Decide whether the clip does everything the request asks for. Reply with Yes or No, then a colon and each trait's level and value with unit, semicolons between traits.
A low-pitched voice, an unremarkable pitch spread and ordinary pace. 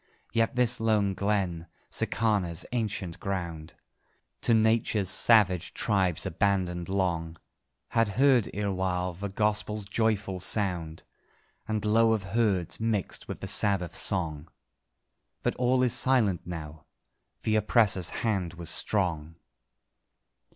No: low, 100 Hz; average, 3.8 semitones; slow, 115 wpm